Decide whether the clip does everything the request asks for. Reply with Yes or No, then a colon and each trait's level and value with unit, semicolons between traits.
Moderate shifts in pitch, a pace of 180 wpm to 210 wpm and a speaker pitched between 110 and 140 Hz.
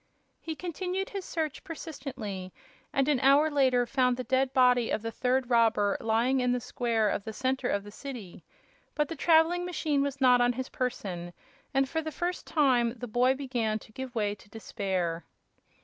No: average, 4.0 semitones; average, 185 wpm; very high, 255 Hz